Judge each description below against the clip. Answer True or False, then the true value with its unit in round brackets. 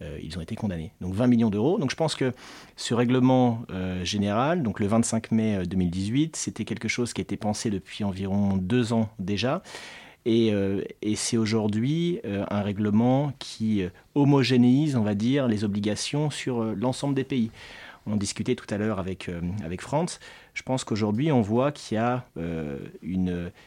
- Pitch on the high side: False (110 Hz)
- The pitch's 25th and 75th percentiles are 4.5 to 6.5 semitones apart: False (4.0 semitones)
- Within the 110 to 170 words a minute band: False (185 wpm)